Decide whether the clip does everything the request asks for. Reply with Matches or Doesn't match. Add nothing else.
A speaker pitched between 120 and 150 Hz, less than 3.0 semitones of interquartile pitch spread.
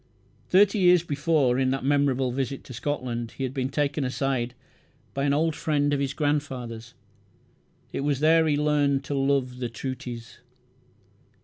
Matches